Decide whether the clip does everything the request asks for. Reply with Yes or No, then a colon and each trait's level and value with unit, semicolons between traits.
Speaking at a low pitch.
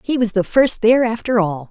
No: high, 220 Hz